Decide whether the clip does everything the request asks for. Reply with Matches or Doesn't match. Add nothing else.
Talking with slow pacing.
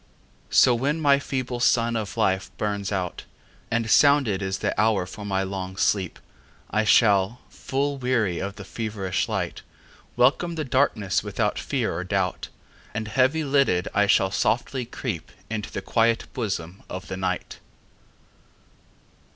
Matches